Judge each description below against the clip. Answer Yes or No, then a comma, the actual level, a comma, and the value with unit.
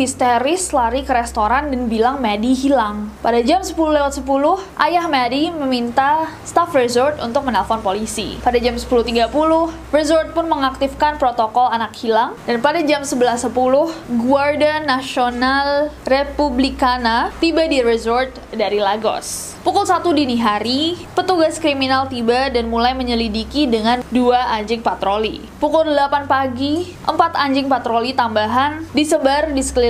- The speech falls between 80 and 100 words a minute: No, average, 130 wpm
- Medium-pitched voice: No, very high, 265 Hz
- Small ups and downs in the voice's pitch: No, average, 3.8 semitones